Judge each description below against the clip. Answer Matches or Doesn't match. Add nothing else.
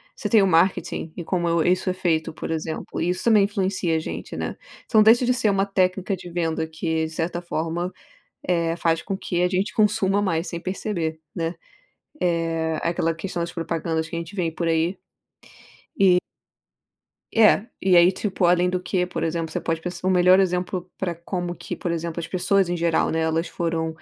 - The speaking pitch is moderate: Matches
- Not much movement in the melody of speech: Matches